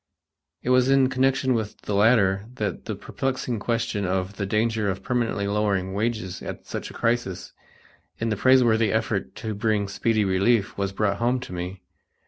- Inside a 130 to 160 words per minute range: No, average, 170 wpm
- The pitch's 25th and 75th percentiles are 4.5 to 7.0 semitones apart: No, average, 3.3 semitones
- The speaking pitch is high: No, low, 110 Hz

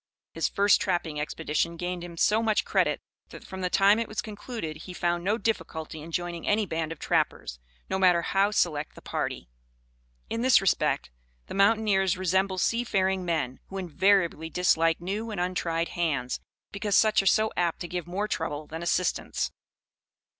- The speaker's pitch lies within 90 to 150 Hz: No, medium, 180 Hz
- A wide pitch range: No, average, 3.5 semitones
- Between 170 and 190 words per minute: Yes, average, 175 wpm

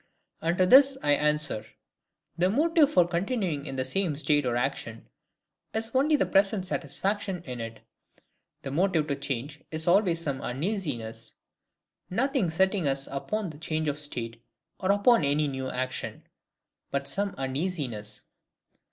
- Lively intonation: Yes, wide, 6.3 semitones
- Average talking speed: Yes, average, 145 wpm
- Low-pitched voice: No, medium, 155 Hz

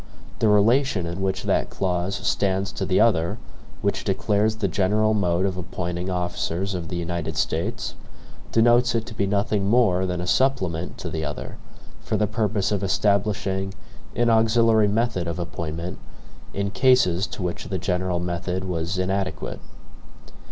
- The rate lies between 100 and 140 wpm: No, average, 155 wpm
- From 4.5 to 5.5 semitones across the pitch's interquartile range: No, average, 3.3 semitones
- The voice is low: Yes, very low, 95 Hz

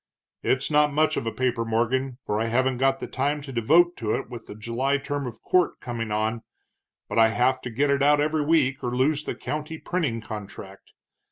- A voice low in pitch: Yes, low, 130 Hz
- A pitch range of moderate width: Yes, average, 4.1 semitones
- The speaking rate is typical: No, fast, 210 wpm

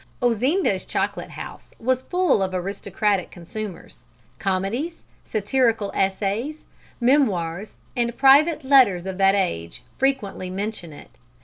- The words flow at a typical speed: No, slow, 110 wpm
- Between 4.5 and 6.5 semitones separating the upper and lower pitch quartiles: Yes, wide, 5.5 semitones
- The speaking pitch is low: No, high, 210 Hz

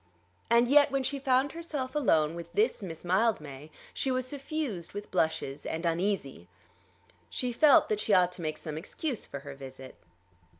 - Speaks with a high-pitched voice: Yes, high, 205 Hz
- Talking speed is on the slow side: No, average, 170 wpm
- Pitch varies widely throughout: Yes, wide, 9.0 semitones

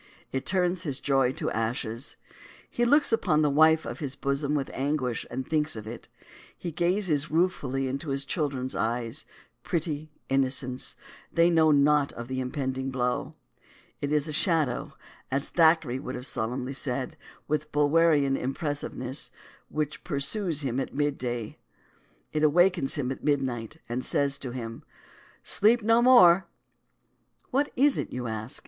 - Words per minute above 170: No, average, 155 wpm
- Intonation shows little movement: No, average, 3.6 semitones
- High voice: No, medium, 140 Hz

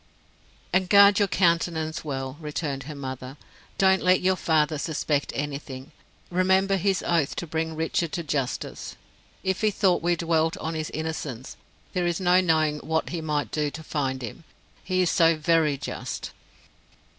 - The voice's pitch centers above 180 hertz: No, medium, 160 Hz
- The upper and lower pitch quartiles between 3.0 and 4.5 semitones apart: Yes, average, 3.3 semitones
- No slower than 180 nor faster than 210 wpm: No, average, 160 wpm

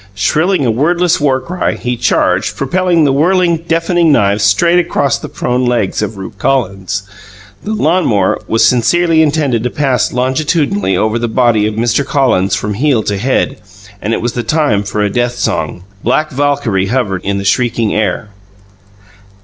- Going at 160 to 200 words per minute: Yes, average, 170 wpm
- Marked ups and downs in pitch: Yes, wide, 6.4 semitones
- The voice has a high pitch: No, low, 125 Hz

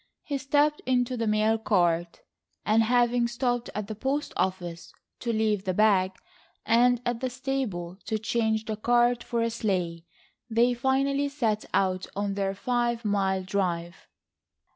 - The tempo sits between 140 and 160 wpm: Yes, average, 150 wpm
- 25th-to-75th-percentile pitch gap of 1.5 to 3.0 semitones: No, average, 4.0 semitones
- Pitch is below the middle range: No, high, 220 Hz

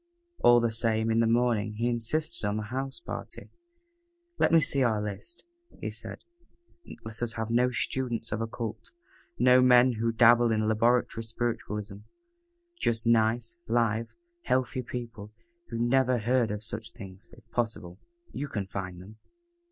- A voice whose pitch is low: Yes, low, 115 Hz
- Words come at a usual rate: Yes, average, 150 wpm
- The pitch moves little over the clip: Yes, narrow, 1.9 semitones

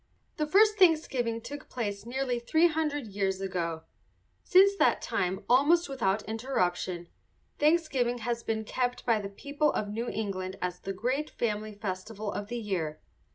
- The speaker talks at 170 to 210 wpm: No, average, 155 wpm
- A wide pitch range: Yes, wide, 6.2 semitones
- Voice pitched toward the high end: Yes, high, 230 Hz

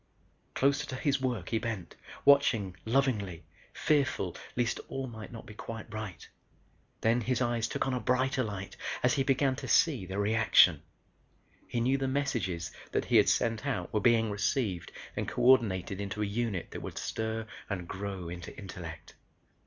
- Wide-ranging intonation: No, average, 4.8 semitones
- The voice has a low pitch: Yes, low, 115 Hz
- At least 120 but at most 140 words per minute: No, average, 170 wpm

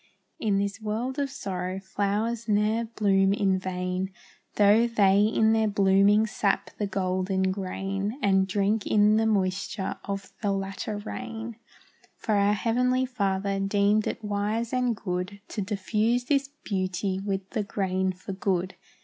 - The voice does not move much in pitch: Yes, narrow, 2.3 semitones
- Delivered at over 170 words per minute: No, average, 145 wpm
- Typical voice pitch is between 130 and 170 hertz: No, high, 200 Hz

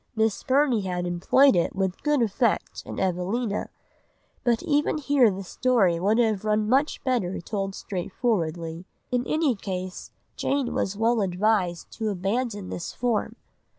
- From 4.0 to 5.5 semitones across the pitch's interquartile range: Yes, average, 4.8 semitones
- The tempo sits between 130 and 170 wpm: Yes, average, 145 wpm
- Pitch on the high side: Yes, high, 210 Hz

